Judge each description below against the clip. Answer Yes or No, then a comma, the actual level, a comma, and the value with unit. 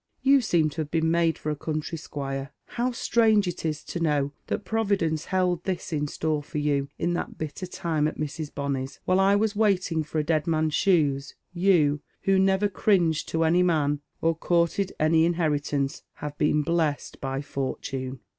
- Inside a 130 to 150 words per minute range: No, average, 185 wpm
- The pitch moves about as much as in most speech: Yes, average, 3.6 semitones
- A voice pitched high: No, medium, 160 Hz